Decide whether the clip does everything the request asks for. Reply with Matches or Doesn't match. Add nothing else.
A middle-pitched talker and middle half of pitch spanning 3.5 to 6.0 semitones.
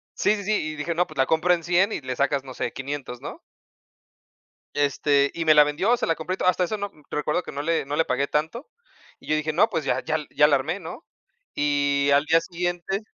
Matches